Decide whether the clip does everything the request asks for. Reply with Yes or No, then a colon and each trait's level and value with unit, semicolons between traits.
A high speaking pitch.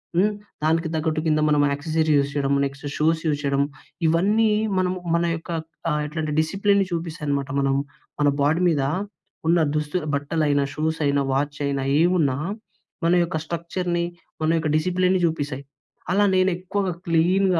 No: medium, 160 Hz